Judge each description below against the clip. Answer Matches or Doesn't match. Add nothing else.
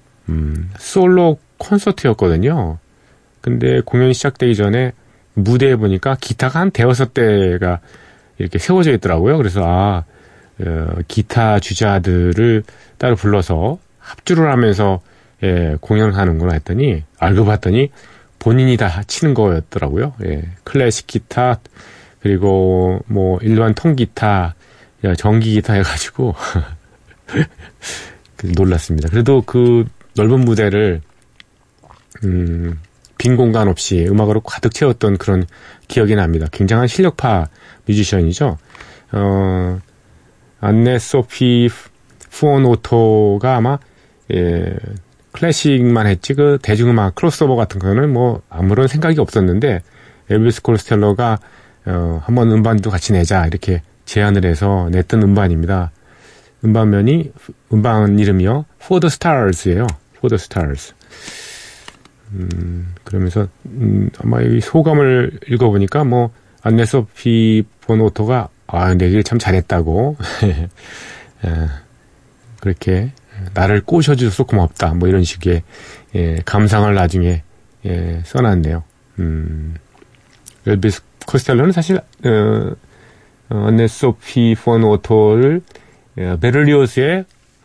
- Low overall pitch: Matches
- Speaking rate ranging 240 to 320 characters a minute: Matches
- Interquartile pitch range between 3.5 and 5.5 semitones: Matches